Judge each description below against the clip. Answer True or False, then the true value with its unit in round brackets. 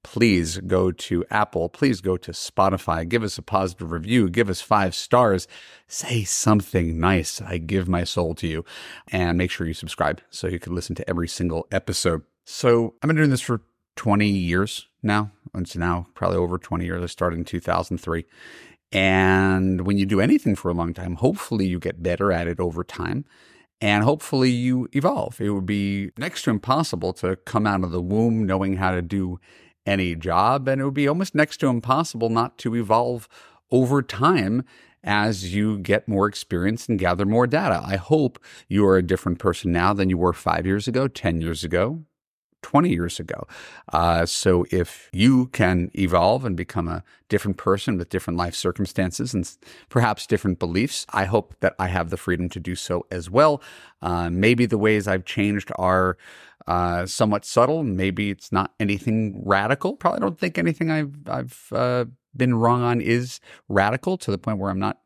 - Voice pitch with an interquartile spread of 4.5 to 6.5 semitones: True (4.8 semitones)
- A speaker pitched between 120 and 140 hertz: False (100 Hz)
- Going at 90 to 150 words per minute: False (185 wpm)